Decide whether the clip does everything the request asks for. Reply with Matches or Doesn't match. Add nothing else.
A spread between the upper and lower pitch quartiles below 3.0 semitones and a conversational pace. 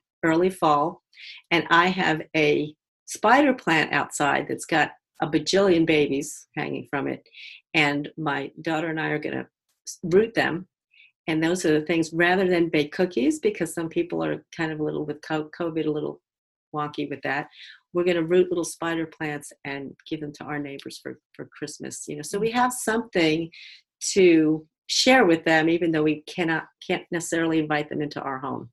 Matches